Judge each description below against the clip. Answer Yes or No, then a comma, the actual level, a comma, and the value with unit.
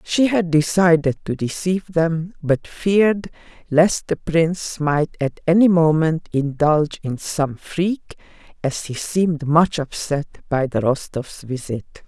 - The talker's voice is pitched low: No, medium, 160 Hz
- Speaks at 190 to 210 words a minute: No, average, 140 wpm